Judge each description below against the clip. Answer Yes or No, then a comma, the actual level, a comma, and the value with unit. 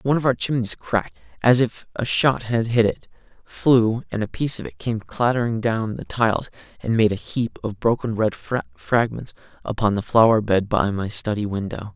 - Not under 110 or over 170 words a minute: No, average, 195 wpm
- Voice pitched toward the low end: Yes, low, 115 Hz